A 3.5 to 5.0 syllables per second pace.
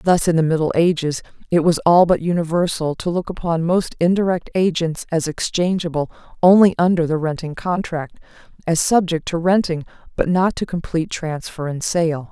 No: 5.2 syllables/s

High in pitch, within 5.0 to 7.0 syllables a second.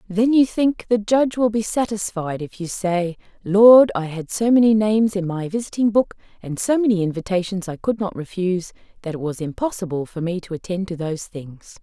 Yes: high, 195 Hz; 5.4 syllables/s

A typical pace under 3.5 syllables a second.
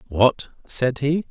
Yes: 3.1 syllables/s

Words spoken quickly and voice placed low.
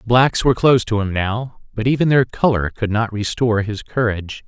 Yes: fast, 215 wpm; low, 115 Hz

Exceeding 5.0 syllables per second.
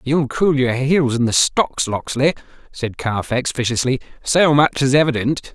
No: 4.4 syllables/s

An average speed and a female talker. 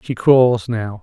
No: average, 175 wpm; male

